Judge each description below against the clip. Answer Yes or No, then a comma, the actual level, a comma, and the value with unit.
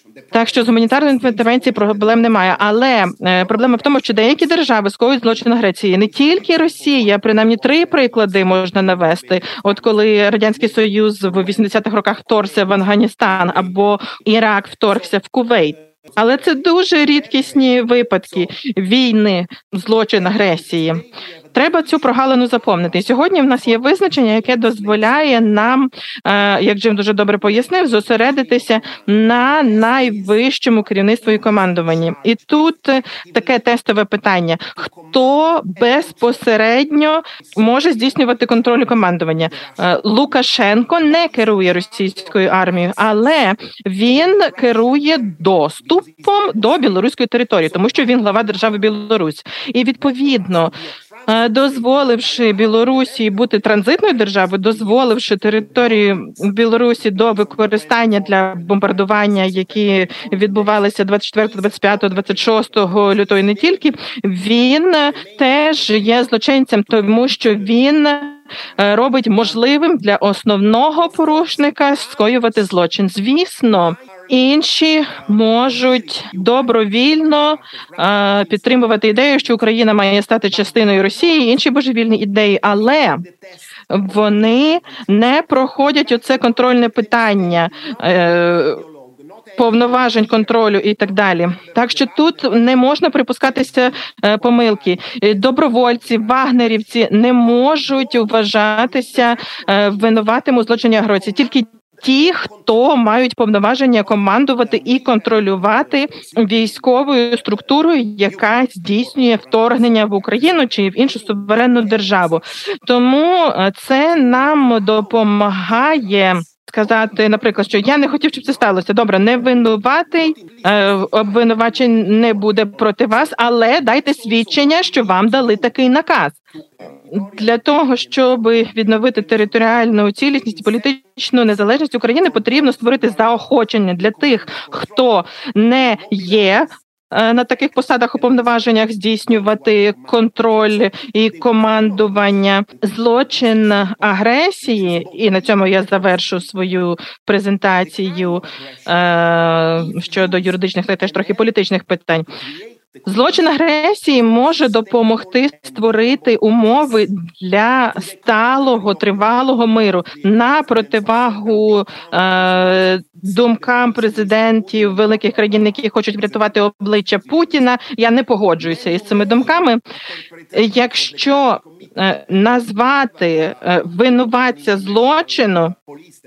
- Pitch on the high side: Yes, high, 225 Hz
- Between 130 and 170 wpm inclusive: No, slow, 105 wpm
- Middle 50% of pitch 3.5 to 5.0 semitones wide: Yes, average, 3.8 semitones